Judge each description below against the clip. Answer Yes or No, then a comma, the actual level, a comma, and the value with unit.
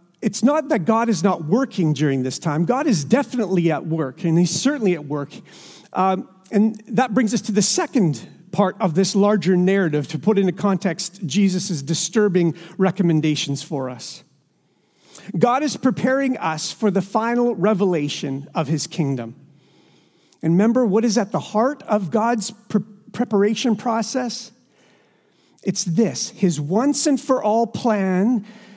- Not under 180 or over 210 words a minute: No, average, 150 wpm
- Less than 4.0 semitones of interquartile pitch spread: No, average, 5.2 semitones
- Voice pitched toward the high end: Yes, high, 200 Hz